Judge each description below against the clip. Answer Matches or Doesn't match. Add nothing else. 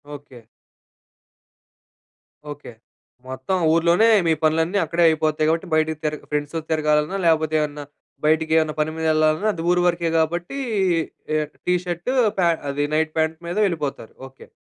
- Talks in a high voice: Doesn't match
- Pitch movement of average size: Doesn't match